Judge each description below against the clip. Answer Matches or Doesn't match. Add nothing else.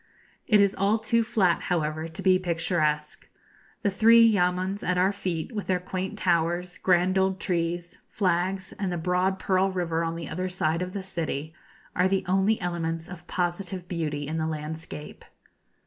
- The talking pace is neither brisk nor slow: Matches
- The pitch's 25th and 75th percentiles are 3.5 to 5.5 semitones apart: Doesn't match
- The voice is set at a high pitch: Doesn't match